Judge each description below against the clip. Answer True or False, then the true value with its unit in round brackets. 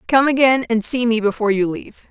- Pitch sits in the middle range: False (230 Hz)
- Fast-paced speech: True (230 wpm)